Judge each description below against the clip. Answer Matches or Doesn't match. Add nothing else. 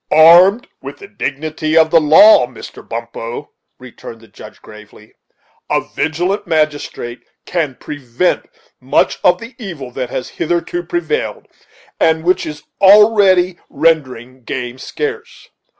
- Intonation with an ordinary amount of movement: Doesn't match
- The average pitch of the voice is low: Doesn't match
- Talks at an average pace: Doesn't match